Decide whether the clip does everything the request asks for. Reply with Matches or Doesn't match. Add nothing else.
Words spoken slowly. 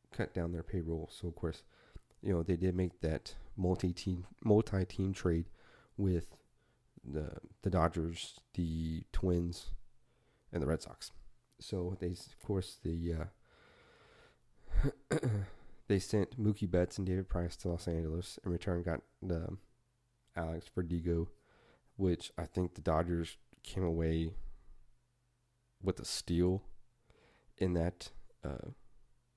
Matches